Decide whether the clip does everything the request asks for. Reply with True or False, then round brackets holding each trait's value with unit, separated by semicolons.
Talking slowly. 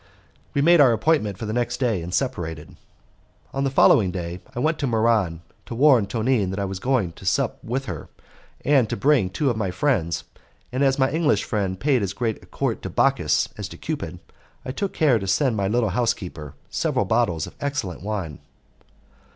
False (195 wpm)